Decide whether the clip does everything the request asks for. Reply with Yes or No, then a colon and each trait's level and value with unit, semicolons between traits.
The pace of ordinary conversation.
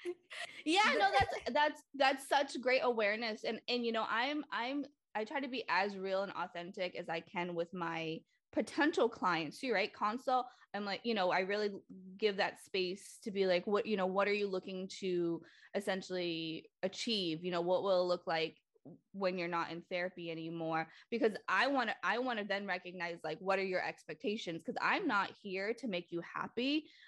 Yes: average, 195 wpm